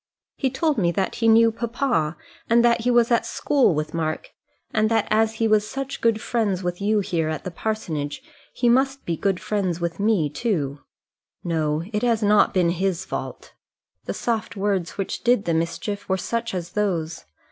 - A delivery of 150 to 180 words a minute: No, average, 190 wpm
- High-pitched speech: Yes, high, 205 Hz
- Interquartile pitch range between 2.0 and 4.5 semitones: No, average, 5.2 semitones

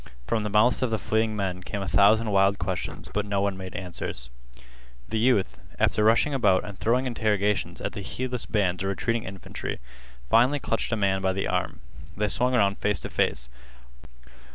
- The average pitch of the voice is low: Yes, low, 105 Hz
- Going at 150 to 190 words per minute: Yes, average, 185 wpm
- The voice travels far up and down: No, average, 2.7 semitones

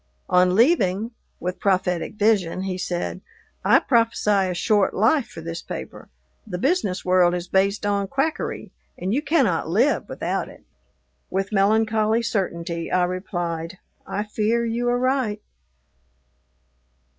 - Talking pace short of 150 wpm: Yes, slow, 135 wpm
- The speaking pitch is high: Yes, high, 200 Hz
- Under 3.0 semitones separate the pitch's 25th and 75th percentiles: No, average, 3.9 semitones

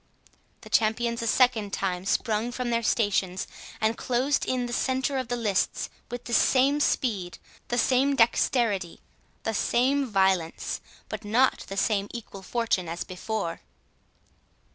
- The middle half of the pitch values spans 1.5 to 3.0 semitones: No, average, 4.0 semitones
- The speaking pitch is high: Yes, high, 230 Hz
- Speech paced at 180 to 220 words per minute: No, average, 140 wpm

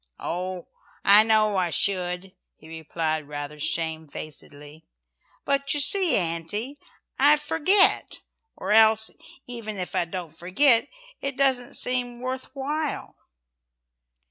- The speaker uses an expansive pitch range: Yes, wide, 7.9 semitones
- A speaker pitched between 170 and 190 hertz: No, high, 210 Hz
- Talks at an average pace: No, slow, 115 wpm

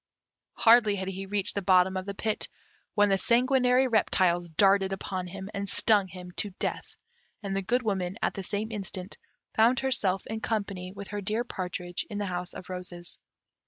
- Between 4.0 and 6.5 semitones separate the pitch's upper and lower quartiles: No, average, 2.7 semitones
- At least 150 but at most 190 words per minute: Yes, average, 185 wpm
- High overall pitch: Yes, high, 195 Hz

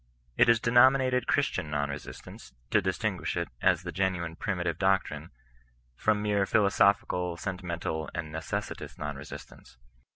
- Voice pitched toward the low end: Yes, very low, 95 Hz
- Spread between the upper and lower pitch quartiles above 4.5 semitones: No, average, 4.0 semitones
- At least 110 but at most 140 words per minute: Yes, slow, 135 wpm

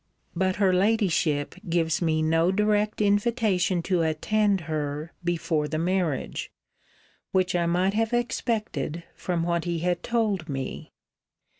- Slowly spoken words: Yes, slow, 130 wpm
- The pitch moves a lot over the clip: No, average, 4.1 semitones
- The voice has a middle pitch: Yes, medium, 175 Hz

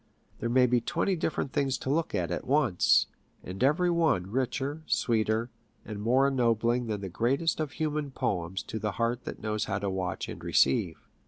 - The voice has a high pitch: No, low, 120 Hz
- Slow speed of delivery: No, average, 185 wpm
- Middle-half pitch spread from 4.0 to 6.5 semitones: Yes, average, 5.1 semitones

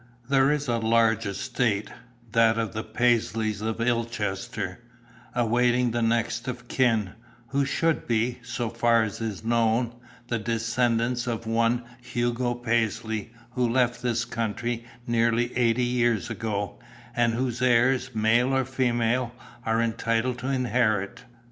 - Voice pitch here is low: Yes, low, 115 Hz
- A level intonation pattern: Yes, narrow, 1.5 semitones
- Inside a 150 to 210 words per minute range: No, slow, 135 wpm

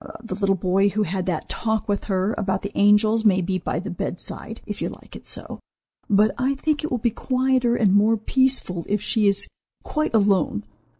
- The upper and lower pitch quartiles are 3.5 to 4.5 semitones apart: No, average, 3.0 semitones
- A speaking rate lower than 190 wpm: No, average, 200 wpm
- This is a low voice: No, high, 210 Hz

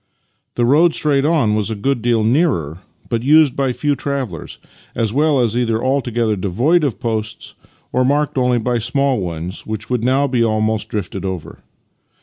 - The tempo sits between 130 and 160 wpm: No, average, 170 wpm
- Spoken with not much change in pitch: No, average, 4.2 semitones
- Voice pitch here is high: No, low, 120 Hz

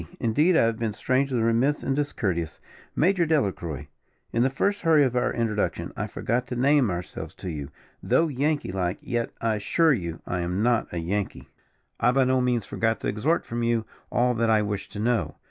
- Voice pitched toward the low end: Yes, low, 115 Hz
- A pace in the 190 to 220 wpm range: Yes, average, 195 wpm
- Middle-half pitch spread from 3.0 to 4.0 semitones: No, average, 4.6 semitones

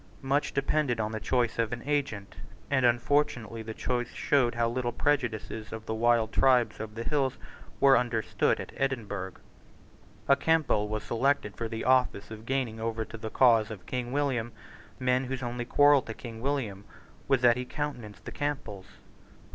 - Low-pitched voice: Yes, low, 120 Hz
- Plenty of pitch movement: No, average, 3.2 semitones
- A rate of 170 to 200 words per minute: Yes, average, 175 wpm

